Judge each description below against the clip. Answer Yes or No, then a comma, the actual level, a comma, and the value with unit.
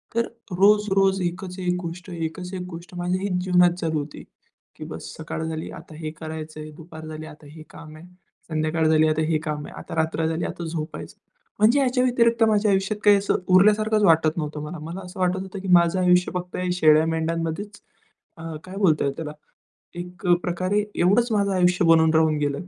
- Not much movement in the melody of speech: No, average, 3.3 semitones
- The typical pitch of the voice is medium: Yes, medium, 175 Hz